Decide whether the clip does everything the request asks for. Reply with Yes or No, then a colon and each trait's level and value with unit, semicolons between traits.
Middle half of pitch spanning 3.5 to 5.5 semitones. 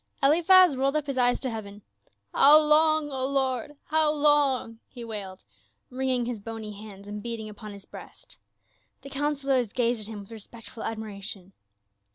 Yes: average, 4.8 semitones